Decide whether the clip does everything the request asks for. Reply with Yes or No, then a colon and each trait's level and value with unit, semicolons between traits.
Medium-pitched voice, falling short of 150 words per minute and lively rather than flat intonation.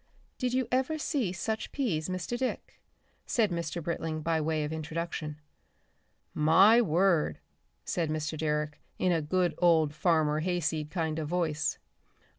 No: medium, 165 Hz; average, 140 wpm; average, 3.1 semitones